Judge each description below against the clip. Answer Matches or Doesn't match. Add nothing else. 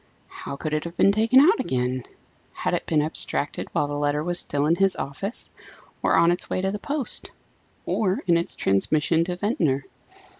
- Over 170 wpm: Matches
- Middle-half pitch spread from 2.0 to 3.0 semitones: Doesn't match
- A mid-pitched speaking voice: Matches